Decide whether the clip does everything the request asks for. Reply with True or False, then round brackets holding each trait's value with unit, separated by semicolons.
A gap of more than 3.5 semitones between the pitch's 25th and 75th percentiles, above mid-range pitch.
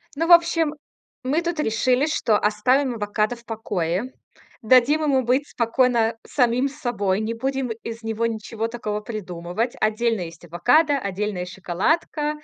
True (4.2 semitones; 230 Hz)